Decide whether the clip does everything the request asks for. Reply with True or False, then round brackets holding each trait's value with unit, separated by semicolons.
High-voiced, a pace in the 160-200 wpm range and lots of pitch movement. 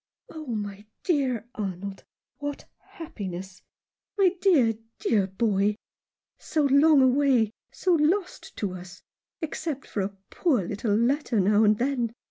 False (230 Hz; 135 wpm; 6.3 semitones)